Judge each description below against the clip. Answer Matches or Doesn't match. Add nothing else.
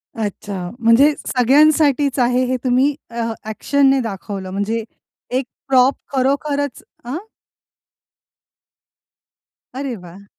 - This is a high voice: Matches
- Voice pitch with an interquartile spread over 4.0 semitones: Doesn't match